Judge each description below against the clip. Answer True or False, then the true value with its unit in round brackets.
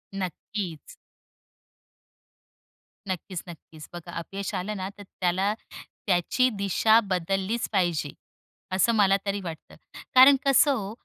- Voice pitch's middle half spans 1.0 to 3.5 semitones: True (2.9 semitones)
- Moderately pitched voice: False (195 Hz)